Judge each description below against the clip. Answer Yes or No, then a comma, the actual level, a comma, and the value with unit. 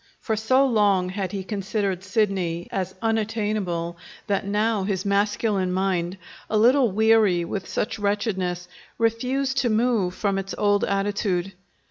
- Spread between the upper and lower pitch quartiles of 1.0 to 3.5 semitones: Yes, average, 2.7 semitones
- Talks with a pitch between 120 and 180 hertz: No, high, 200 Hz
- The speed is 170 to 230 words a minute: No, slow, 135 wpm